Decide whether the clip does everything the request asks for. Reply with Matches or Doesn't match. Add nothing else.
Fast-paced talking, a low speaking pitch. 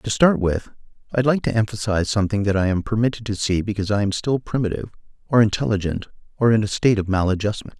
Matches